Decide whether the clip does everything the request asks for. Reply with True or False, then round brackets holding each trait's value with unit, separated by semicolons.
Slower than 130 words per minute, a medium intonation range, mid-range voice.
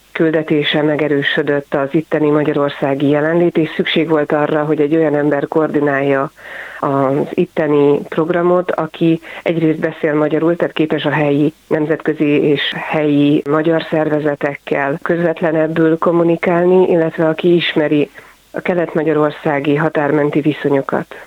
False (115 wpm; 1.8 semitones; 155 Hz)